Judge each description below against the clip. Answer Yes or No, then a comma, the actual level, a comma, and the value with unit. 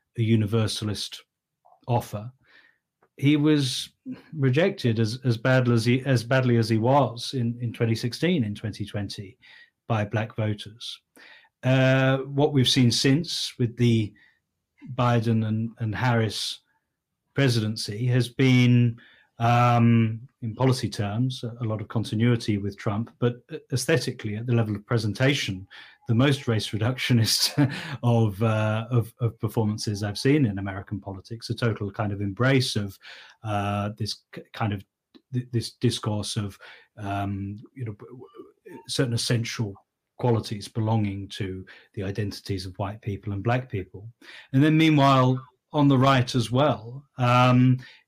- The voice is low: Yes, low, 120 Hz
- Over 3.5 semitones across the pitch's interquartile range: No, average, 3.1 semitones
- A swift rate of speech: No, slow, 135 wpm